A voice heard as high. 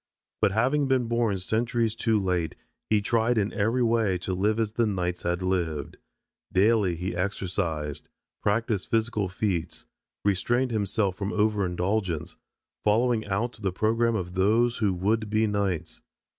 No: low, 105 Hz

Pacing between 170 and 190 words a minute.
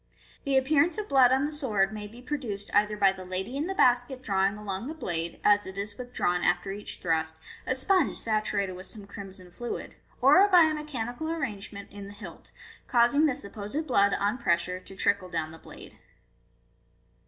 No: average, 200 wpm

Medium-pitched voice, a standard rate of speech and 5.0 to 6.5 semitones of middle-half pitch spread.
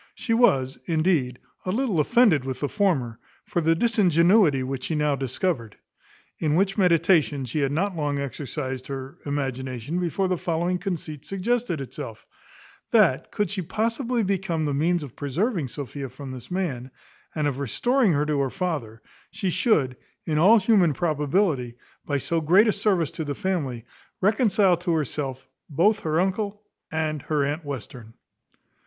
Yes: medium, 160 Hz; average, 160 wpm; wide, 5.6 semitones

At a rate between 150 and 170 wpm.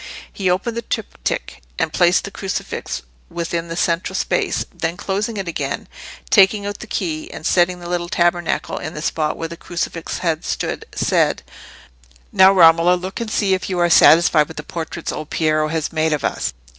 No: average, 185 wpm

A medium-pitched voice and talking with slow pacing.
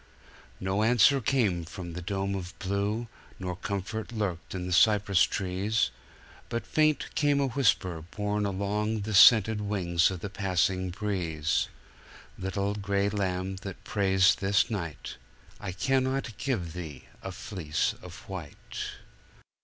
No: low, 100 Hz; slow, 130 wpm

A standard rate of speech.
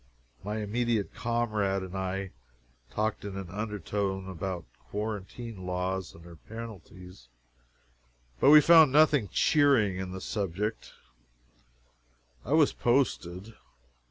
No: slow, 110 wpm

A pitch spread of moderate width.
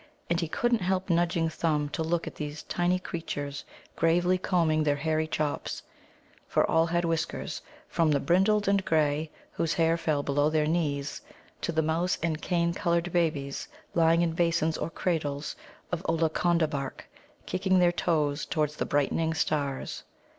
No: narrow, 2.2 semitones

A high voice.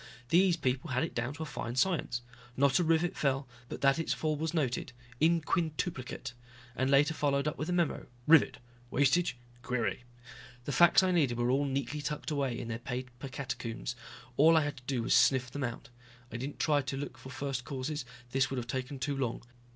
No: medium, 140 Hz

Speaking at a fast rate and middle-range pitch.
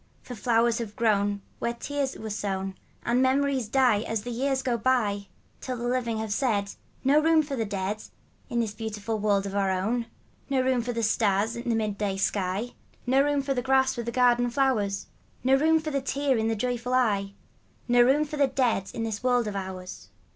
No: fast, 210 wpm; high, 235 Hz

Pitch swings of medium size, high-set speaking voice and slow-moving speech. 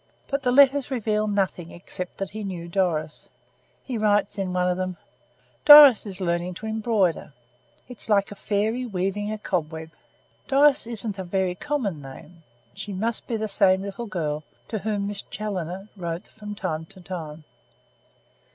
No: average, 3.4 semitones; high, 200 Hz; average, 160 wpm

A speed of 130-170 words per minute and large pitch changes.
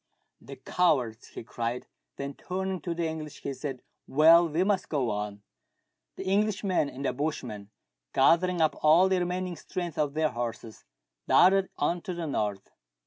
Yes: average, 165 wpm; wide, 5.9 semitones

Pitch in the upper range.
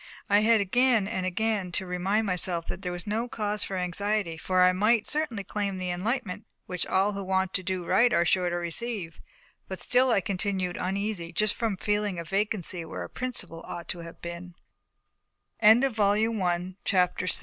Yes: high, 195 Hz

